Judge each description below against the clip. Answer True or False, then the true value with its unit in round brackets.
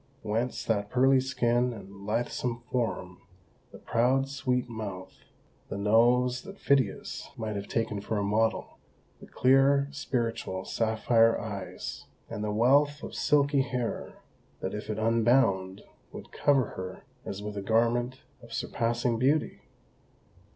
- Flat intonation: False (3.5 semitones)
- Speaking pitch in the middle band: False (115 Hz)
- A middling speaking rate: False (130 wpm)